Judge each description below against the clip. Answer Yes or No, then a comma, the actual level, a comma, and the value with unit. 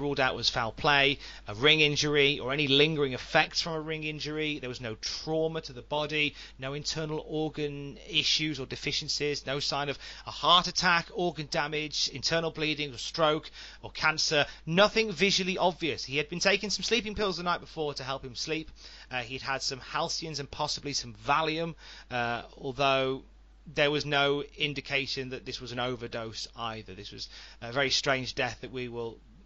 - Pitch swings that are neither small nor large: Yes, average, 3.0 semitones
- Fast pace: No, average, 185 wpm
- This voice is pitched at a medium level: Yes, medium, 145 Hz